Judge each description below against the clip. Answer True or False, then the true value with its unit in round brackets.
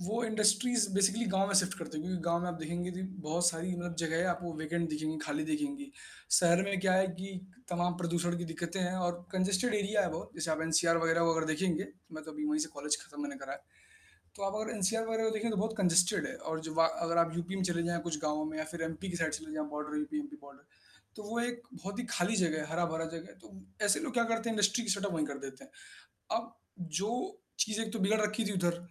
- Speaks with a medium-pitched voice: True (180 Hz)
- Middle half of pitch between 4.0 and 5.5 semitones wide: True (4.5 semitones)